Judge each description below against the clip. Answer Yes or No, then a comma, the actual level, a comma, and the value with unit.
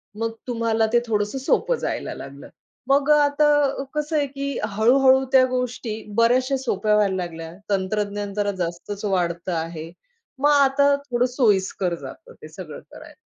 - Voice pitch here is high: Yes, high, 230 Hz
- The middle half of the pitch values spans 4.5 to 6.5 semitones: Yes, average, 5.3 semitones